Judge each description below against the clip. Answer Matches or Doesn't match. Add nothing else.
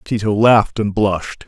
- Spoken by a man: Matches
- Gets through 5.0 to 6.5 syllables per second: Matches